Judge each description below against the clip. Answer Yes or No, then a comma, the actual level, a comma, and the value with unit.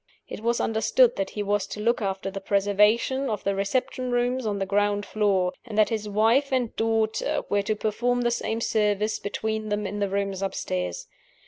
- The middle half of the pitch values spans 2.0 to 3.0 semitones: Yes, narrow, 2.4 semitones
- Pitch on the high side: Yes, high, 210 Hz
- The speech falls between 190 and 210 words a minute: Yes, average, 195 wpm